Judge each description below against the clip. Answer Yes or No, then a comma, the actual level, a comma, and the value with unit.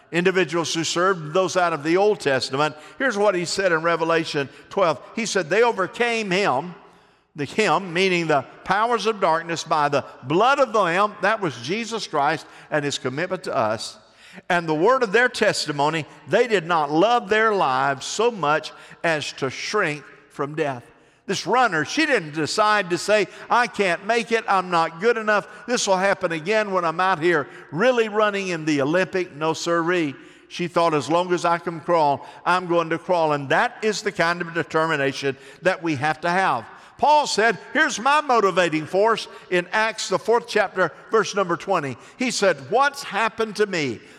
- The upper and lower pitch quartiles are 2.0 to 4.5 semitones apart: No, average, 5.0 semitones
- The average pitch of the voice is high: No, medium, 180 Hz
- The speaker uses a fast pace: No, average, 185 wpm